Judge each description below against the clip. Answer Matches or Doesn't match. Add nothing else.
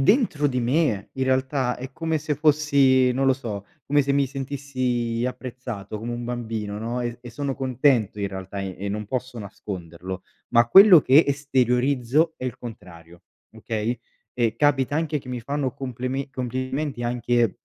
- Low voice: Matches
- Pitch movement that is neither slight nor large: Matches